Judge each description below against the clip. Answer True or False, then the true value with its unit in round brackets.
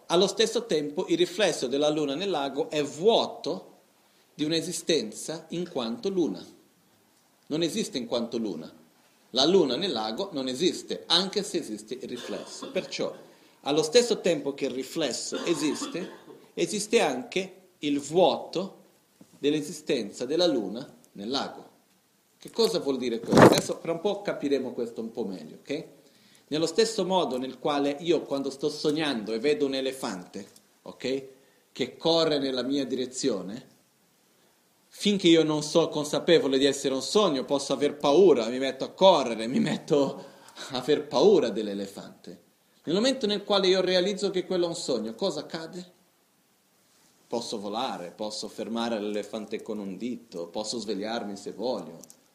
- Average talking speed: True (150 wpm)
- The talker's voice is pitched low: False (150 Hz)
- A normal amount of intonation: False (5.9 semitones)